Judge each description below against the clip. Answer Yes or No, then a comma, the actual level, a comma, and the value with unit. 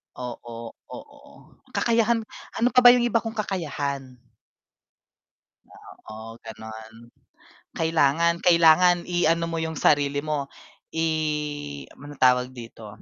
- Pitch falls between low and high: Yes, medium, 145 Hz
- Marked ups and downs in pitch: Yes, wide, 6.0 semitones